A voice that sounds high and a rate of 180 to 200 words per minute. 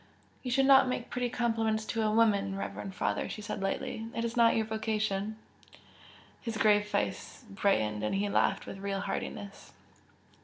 No: high, 215 Hz; average, 165 wpm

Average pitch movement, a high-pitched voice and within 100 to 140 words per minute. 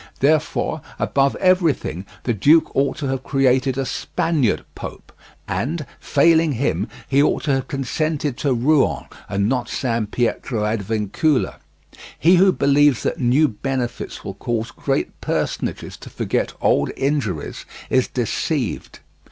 No: average, 3.8 semitones; low, 135 Hz; slow, 135 wpm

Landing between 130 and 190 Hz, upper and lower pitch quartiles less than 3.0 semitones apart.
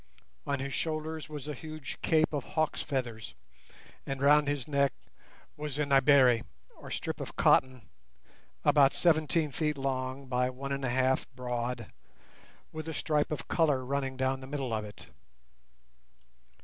Yes: medium, 140 Hz; narrow, 2.6 semitones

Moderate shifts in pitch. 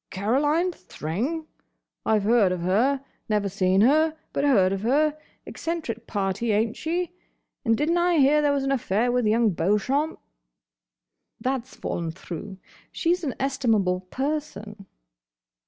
No: wide, 6.6 semitones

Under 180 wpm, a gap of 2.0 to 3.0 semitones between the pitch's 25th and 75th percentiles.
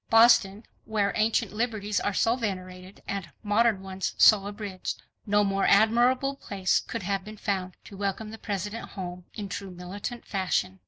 Yes: average, 160 wpm; narrow, 2.4 semitones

